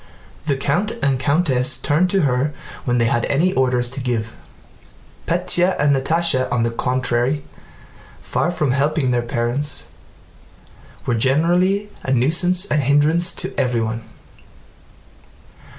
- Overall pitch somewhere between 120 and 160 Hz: Yes, medium, 140 Hz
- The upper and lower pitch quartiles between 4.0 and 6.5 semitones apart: Yes, average, 4.9 semitones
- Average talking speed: No, slow, 130 wpm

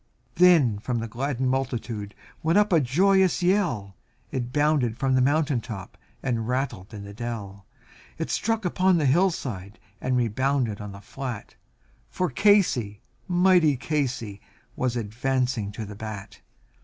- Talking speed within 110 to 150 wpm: Yes, average, 145 wpm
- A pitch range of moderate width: No, wide, 6.1 semitones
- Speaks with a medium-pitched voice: No, low, 130 Hz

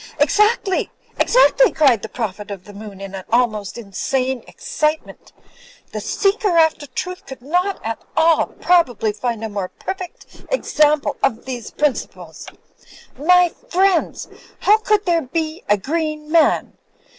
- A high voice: Yes, very high, 300 Hz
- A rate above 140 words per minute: No, slow, 135 wpm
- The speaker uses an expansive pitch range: Yes, wide, 7.9 semitones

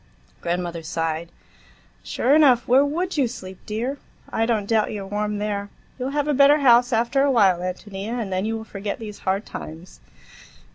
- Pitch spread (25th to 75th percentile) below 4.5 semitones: No, average, 4.8 semitones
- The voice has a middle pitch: No, high, 215 Hz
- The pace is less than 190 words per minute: Yes, average, 165 wpm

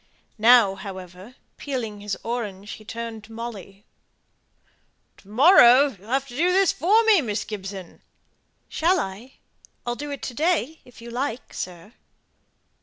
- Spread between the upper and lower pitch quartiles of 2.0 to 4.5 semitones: No, average, 5.2 semitones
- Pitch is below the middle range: No, high, 235 Hz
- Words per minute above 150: No, average, 145 wpm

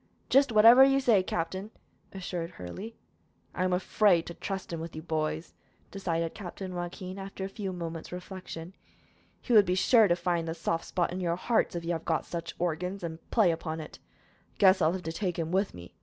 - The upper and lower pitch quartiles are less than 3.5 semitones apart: Yes, average, 2.8 semitones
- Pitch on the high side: No, medium, 180 Hz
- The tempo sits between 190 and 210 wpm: Yes, average, 200 wpm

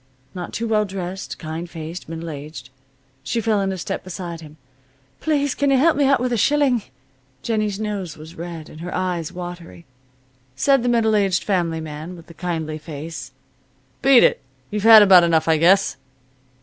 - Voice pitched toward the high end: No, medium, 180 Hz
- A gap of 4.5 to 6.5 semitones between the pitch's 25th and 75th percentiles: Yes, average, 4.9 semitones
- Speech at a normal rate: Yes, average, 175 wpm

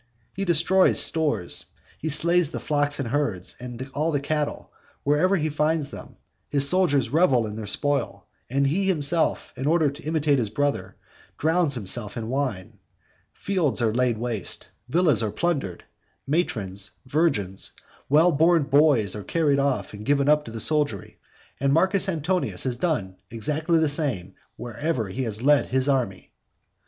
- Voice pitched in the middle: Yes, medium, 145 Hz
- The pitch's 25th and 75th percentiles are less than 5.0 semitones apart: No, average, 5.3 semitones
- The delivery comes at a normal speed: Yes, average, 160 wpm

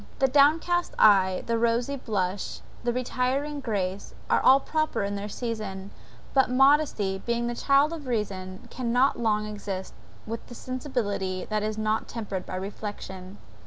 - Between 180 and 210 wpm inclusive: No, average, 150 wpm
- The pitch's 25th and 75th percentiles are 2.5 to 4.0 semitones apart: No, average, 4.5 semitones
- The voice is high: Yes, high, 225 Hz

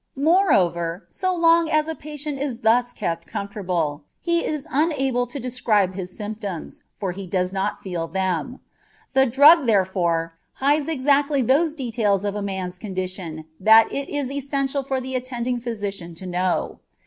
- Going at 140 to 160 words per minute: Yes, average, 155 wpm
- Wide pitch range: Yes, wide, 7.0 semitones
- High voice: Yes, high, 230 Hz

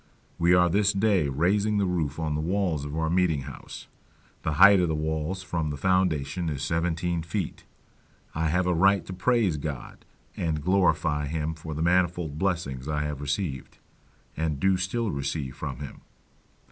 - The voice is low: Yes, very low, 80 Hz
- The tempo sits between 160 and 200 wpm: Yes, average, 170 wpm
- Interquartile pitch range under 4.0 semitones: Yes, average, 3.6 semitones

